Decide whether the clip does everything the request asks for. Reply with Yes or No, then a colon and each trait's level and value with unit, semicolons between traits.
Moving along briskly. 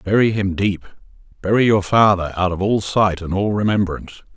No: average, 180 wpm